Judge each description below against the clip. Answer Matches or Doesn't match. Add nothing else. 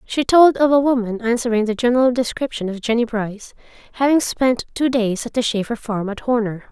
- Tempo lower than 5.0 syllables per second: Doesn't match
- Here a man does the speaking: Doesn't match